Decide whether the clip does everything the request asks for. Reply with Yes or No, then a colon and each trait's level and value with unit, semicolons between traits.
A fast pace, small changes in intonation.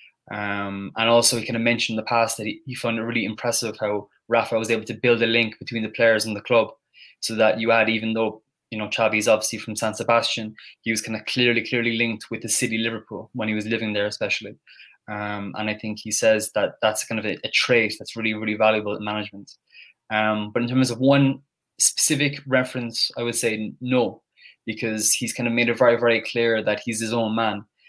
Yes: fast, 230 wpm; narrow, 1.6 semitones